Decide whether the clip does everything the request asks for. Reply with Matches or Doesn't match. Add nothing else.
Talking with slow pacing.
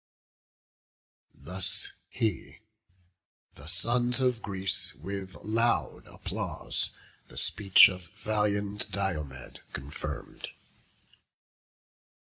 Matches